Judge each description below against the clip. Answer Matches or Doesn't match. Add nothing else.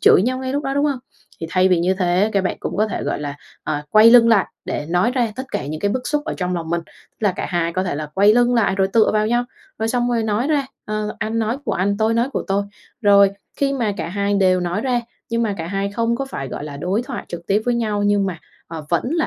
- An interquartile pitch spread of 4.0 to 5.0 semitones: Matches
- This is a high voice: Matches